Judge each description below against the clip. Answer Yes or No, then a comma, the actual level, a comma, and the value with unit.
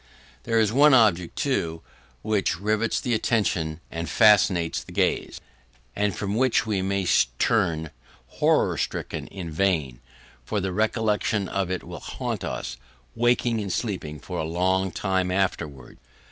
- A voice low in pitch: Yes, very low, 95 Hz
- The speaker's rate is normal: Yes, average, 145 wpm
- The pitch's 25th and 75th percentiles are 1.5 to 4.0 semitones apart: No, average, 4.4 semitones